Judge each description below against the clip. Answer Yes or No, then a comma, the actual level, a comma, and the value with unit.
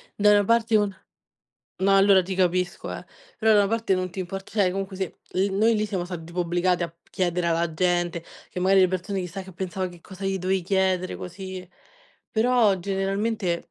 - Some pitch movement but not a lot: No, narrow, 1.8 semitones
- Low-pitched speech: No, high, 190 Hz